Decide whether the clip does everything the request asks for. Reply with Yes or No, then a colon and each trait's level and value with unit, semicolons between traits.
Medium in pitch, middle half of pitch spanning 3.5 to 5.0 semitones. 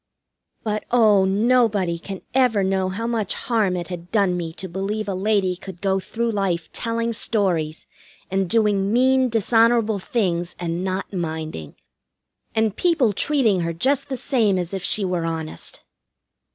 No: high, 200 Hz; average, 4.0 semitones